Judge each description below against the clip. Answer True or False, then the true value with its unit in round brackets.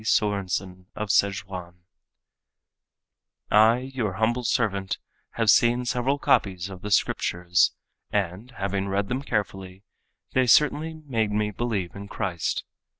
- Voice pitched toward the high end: False (105 Hz)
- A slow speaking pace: True (120 wpm)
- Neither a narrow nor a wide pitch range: True (3.9 semitones)